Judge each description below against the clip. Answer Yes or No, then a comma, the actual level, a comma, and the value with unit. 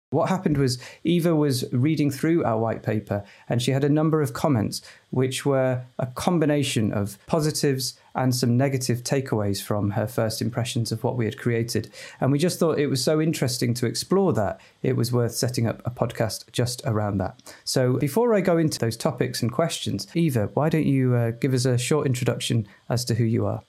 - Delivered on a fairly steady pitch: No, average, 4.2 semitones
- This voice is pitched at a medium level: No, low, 130 Hz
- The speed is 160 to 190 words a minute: No, fast, 205 wpm